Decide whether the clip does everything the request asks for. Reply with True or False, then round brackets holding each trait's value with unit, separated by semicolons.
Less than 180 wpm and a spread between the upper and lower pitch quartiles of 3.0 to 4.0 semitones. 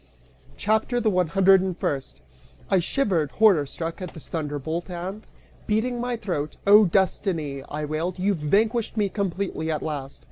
False (155 wpm; 4.9 semitones)